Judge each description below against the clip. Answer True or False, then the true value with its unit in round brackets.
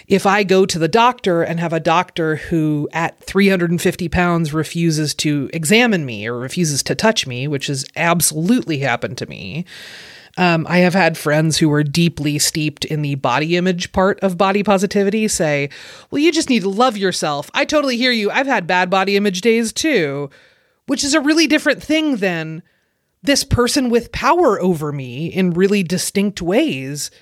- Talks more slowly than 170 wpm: False (180 wpm)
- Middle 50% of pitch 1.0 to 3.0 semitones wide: False (4.8 semitones)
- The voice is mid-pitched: True (180 Hz)